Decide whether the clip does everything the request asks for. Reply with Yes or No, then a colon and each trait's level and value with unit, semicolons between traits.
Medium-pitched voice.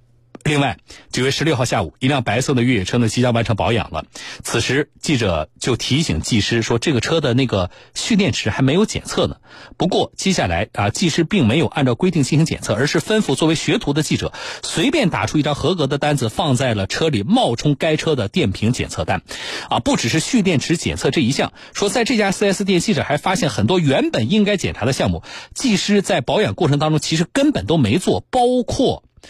Yes: medium, 145 Hz